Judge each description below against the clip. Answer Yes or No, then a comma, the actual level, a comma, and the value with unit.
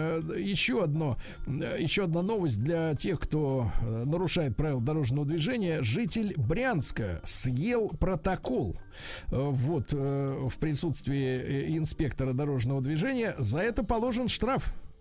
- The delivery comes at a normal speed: No, slow, 105 wpm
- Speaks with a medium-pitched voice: Yes, medium, 150 Hz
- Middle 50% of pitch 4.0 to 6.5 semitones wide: Yes, average, 5.2 semitones